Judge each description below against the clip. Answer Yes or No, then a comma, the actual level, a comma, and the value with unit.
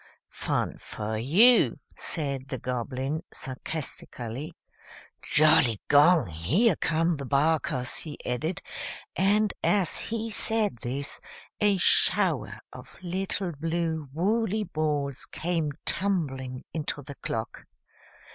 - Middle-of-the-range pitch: Yes, medium, 155 Hz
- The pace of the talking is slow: Yes, slow, 100 wpm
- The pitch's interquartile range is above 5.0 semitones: Yes, wide, 5.4 semitones